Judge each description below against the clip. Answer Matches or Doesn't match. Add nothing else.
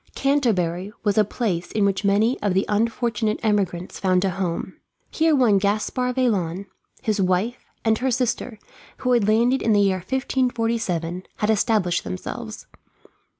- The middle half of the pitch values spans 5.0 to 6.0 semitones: Doesn't match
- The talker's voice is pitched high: Matches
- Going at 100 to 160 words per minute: Matches